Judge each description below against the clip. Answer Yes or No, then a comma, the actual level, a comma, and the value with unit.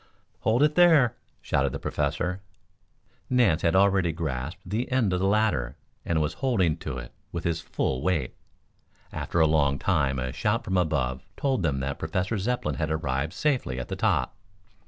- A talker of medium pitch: No, very low, 85 Hz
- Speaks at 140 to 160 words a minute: No, average, 175 wpm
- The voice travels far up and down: Yes, wide, 7.3 semitones